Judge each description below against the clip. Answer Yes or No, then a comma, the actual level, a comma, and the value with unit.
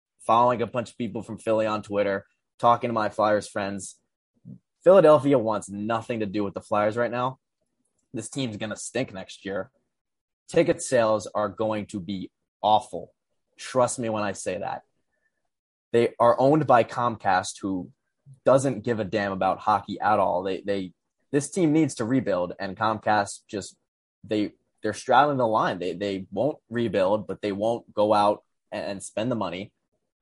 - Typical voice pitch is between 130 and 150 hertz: No, low, 110 Hz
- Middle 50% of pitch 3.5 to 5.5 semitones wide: No, average, 3.0 semitones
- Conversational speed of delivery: Yes, average, 170 wpm